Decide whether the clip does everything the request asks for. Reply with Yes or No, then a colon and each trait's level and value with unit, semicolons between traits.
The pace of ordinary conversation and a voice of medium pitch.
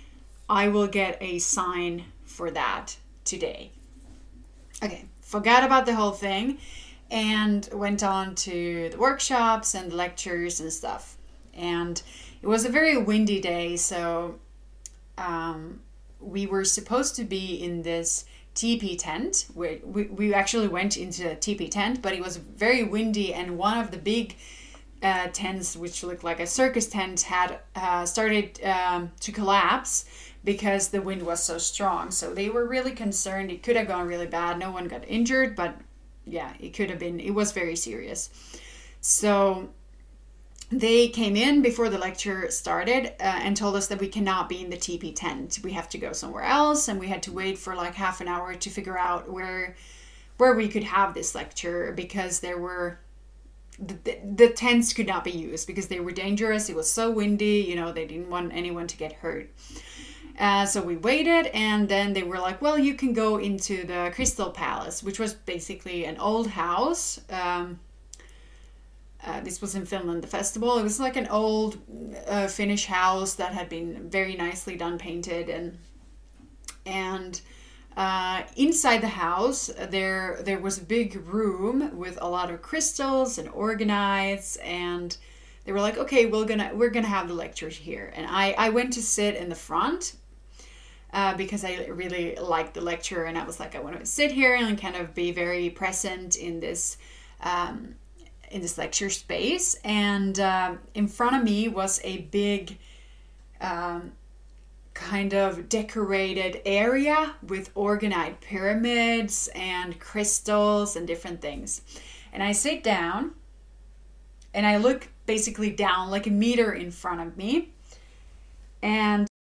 No: average, 170 wpm; high, 195 Hz